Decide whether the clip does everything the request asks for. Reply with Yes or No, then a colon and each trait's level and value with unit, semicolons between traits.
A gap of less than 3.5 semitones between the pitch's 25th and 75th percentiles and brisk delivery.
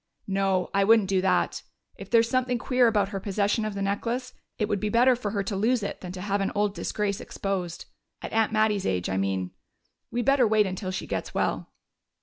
Yes: average, 2.8 semitones; fast, 220 wpm